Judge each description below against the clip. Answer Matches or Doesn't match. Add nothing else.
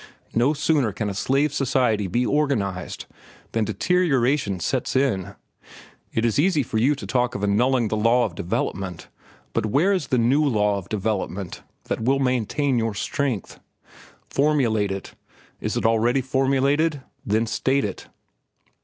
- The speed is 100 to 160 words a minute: Matches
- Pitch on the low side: Matches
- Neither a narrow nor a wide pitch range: Matches